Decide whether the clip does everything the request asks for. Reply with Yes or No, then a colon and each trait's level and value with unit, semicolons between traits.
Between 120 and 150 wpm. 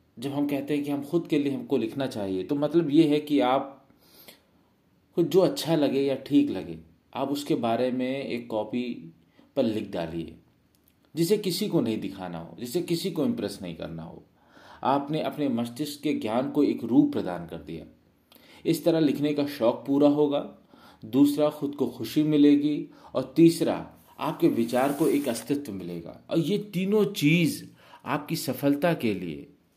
No: average, 175 wpm